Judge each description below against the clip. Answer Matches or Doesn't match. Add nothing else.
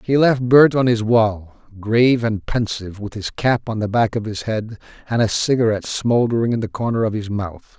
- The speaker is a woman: Doesn't match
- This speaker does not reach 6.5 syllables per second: Matches